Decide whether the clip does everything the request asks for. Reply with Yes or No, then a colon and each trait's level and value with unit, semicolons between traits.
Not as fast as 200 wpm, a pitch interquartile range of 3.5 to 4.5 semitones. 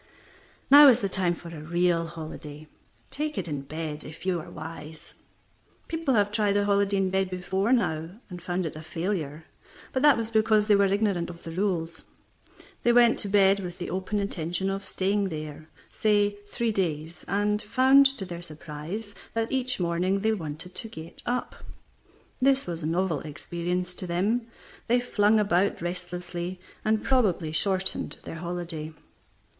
Yes: average, 170 wpm; average, 3.9 semitones